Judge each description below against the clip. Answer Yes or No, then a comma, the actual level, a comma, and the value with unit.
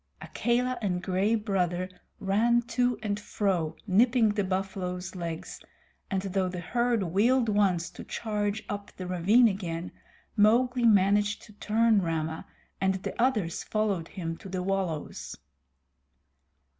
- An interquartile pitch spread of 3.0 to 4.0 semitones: Yes, average, 3.4 semitones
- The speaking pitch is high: Yes, high, 200 Hz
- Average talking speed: No, slow, 130 wpm